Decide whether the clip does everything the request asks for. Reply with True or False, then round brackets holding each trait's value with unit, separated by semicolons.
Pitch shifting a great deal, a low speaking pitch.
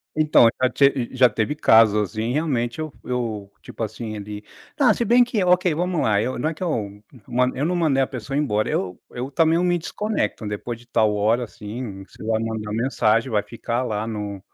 True (5.9 semitones; 120 Hz)